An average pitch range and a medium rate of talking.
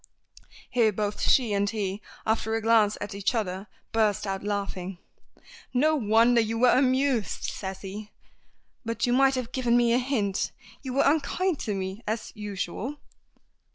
Yes: average, 3.6 semitones; average, 155 wpm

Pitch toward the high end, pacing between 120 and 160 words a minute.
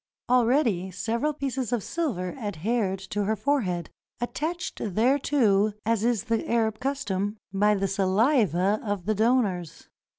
Yes: high, 220 Hz; slow, 135 wpm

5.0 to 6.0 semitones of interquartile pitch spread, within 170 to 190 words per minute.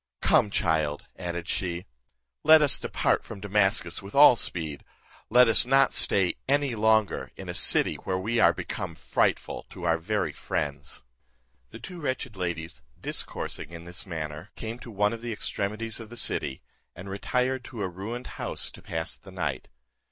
Yes: wide, 5.4 semitones; average, 175 wpm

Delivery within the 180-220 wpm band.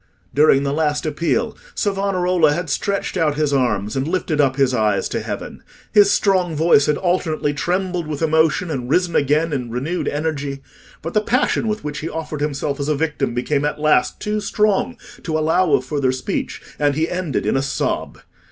Yes: average, 190 wpm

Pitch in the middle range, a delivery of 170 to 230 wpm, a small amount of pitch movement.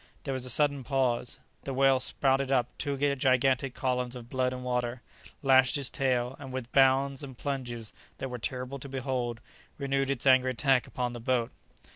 No: low, 130 Hz; average, 180 wpm; narrow, 1.6 semitones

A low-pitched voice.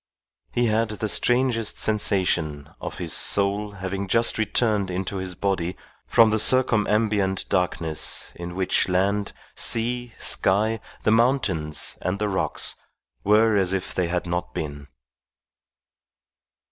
Yes: low, 100 Hz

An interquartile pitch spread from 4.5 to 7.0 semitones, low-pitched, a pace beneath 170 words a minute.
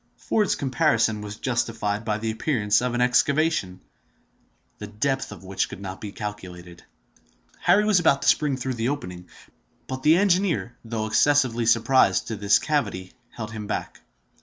Yes: average, 4.9 semitones; low, 115 Hz; average, 160 wpm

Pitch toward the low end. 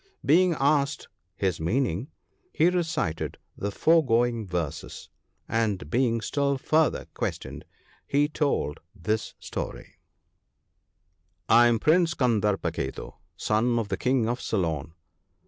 Yes: low, 120 Hz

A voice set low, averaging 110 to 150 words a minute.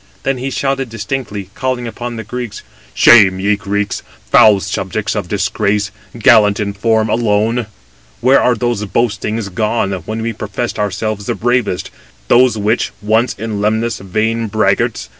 Yes: low, 110 Hz; average, 145 wpm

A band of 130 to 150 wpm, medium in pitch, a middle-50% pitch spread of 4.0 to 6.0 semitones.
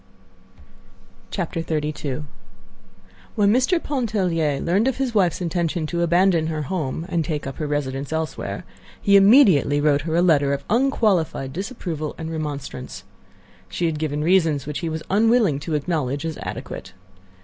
Yes: average, 145 wpm; medium, 160 Hz; average, 4.4 semitones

